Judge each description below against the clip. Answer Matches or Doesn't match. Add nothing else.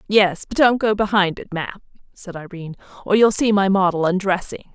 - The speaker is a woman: Matches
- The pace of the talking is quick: Doesn't match